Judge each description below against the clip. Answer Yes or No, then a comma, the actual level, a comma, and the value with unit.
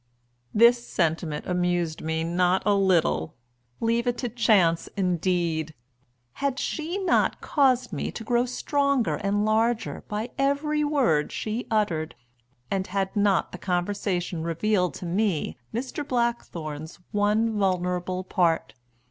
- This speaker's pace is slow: Yes, slow, 125 wpm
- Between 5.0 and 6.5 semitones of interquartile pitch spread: Yes, average, 5.3 semitones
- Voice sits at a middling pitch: No, high, 200 Hz